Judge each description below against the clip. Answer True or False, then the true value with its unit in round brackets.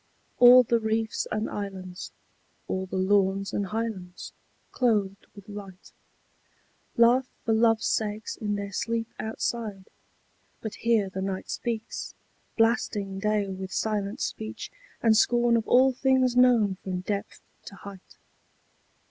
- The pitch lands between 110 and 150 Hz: False (215 Hz)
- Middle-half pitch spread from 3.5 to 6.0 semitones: False (2.9 semitones)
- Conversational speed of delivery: False (130 wpm)